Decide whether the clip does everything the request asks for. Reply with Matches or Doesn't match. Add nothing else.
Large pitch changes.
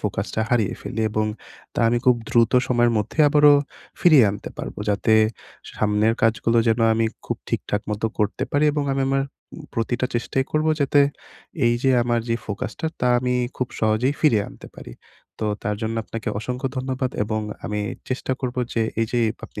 Doesn't match